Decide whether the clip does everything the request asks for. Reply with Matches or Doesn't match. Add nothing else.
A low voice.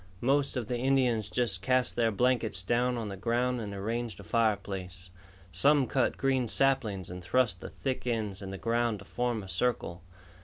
Matches